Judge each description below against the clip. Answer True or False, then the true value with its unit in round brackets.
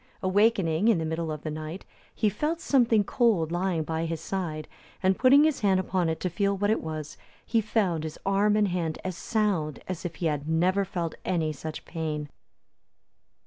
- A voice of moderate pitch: True (180 Hz)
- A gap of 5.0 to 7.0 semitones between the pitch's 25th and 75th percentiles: False (4.3 semitones)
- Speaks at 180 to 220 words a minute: True (190 wpm)